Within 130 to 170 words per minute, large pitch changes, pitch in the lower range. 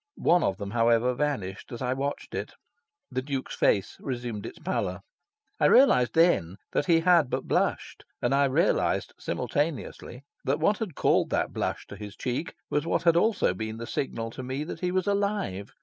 No: average, 185 wpm; wide, 6.4 semitones; low, 130 Hz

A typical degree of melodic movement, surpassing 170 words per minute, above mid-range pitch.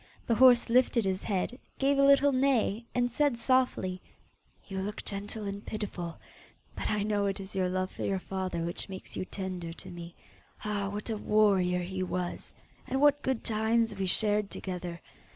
Yes: average, 4.0 semitones; average, 180 wpm; high, 205 Hz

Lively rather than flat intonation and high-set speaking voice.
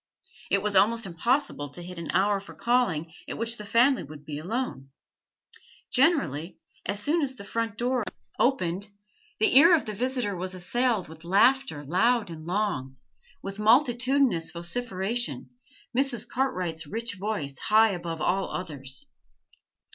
Yes: wide, 6.2 semitones; high, 205 Hz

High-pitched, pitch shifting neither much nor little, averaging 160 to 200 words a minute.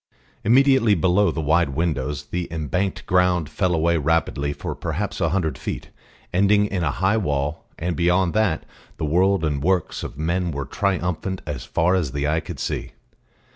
No: very low, 85 Hz; average, 3.6 semitones; average, 170 wpm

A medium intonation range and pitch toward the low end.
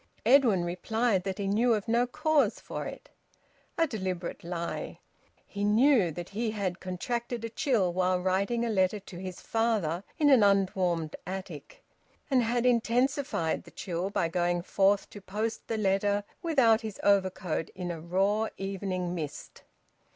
No: average, 4.1 semitones; high, 200 Hz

